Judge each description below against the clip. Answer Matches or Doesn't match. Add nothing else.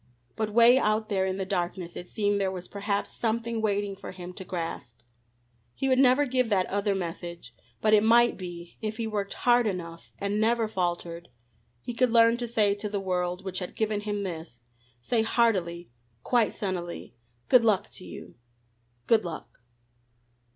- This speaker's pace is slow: Doesn't match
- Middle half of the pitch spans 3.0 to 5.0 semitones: Matches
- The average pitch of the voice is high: Matches